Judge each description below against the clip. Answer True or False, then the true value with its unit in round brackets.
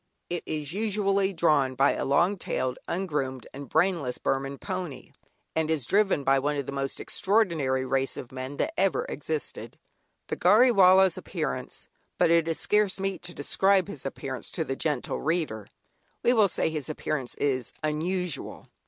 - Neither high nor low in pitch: True (160 Hz)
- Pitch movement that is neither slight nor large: False (5.8 semitones)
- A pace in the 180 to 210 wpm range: False (165 wpm)